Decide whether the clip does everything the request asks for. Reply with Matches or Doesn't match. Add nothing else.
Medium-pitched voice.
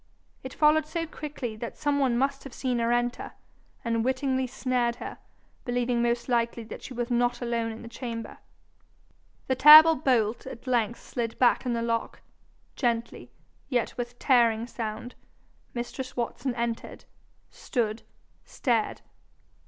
Doesn't match